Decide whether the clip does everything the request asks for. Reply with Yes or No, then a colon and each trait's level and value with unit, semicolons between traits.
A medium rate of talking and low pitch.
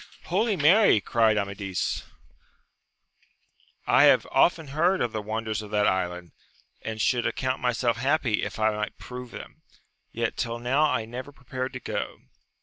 Yes: average, 150 wpm; low, 120 Hz